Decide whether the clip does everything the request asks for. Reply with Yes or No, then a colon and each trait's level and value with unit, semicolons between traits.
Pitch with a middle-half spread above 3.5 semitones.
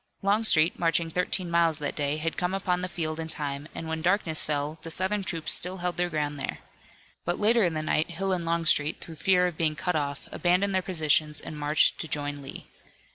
No: average, 2.8 semitones